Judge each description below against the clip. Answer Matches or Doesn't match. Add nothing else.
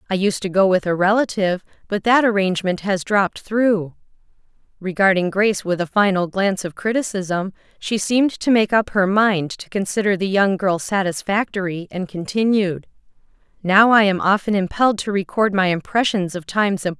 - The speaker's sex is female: Matches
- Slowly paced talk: Doesn't match